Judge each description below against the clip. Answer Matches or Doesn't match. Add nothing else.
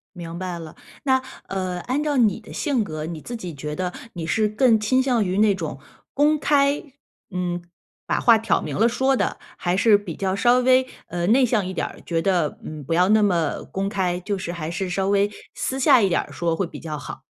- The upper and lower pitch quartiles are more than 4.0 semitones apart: Matches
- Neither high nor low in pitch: Doesn't match